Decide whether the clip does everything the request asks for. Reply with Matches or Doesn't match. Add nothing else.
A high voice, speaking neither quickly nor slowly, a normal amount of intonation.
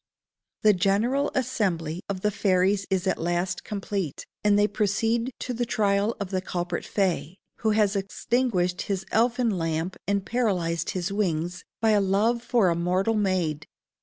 Matches